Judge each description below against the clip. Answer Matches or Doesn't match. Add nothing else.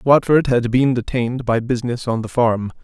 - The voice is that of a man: Matches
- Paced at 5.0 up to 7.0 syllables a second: Matches